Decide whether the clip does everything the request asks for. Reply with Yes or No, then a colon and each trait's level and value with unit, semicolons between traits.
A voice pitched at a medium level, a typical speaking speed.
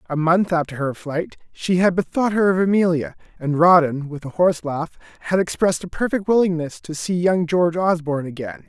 Yes: medium, 170 Hz; average, 195 wpm